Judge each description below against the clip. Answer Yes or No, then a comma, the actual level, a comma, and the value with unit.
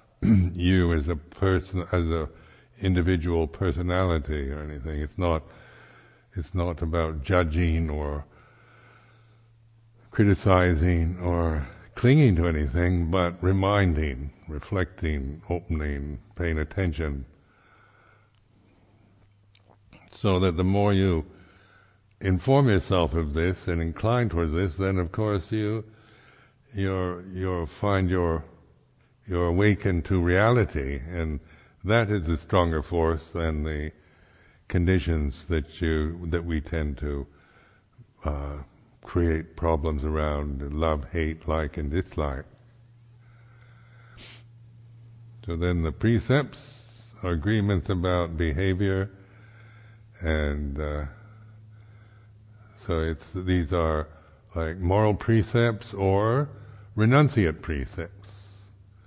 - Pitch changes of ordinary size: Yes, average, 4.9 semitones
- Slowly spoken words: Yes, slow, 100 wpm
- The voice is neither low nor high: No, very low, 90 Hz